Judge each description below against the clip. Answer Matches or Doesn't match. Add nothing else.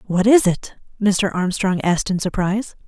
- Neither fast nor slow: Matches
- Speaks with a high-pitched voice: Matches